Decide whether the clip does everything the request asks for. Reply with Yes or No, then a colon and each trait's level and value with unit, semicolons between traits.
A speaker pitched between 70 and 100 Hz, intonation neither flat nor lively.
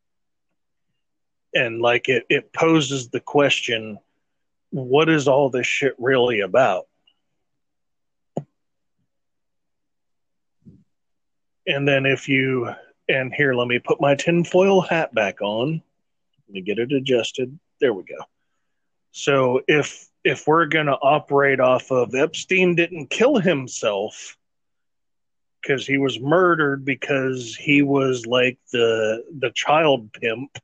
No: low, 135 Hz; average, 3.0 semitones